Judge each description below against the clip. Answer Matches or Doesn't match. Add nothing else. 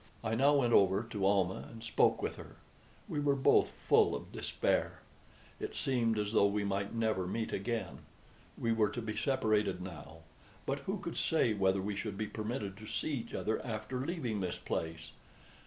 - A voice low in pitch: Matches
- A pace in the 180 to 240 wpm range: Matches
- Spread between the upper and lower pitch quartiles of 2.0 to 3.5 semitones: Matches